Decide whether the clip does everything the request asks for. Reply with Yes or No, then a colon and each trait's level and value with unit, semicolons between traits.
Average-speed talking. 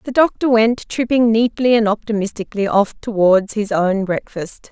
Yes: average, 155 wpm